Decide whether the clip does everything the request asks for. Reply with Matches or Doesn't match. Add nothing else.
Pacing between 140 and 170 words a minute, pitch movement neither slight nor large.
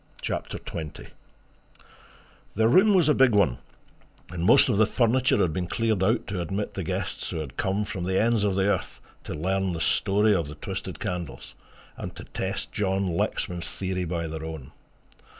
Doesn't match